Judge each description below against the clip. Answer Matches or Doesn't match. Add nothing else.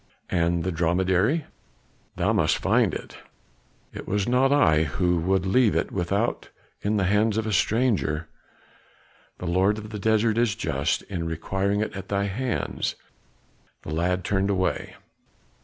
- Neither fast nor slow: Matches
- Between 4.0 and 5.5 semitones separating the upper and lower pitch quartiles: Doesn't match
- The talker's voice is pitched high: Doesn't match